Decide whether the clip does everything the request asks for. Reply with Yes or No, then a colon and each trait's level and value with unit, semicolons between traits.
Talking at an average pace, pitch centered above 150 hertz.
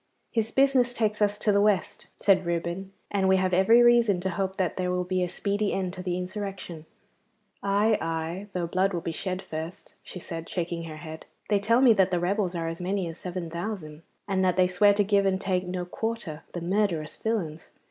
No: fast, 215 wpm; medium, 185 Hz